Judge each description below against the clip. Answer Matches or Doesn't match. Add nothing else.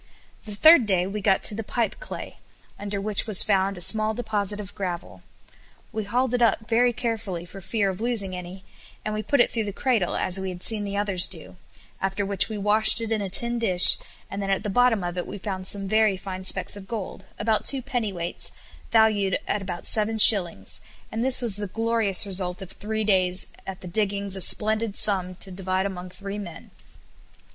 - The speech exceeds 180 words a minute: Matches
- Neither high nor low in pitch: Doesn't match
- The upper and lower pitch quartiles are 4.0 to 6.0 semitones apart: Doesn't match